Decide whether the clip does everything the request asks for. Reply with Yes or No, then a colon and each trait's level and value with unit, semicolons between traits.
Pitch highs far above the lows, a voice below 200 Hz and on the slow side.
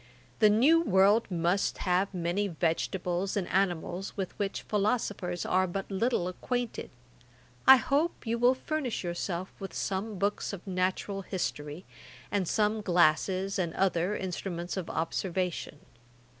No: average, 2.8 semitones; high, 190 Hz; slow, 130 wpm